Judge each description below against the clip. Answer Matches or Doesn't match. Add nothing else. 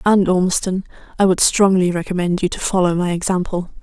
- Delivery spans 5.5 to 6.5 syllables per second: Matches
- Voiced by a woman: Matches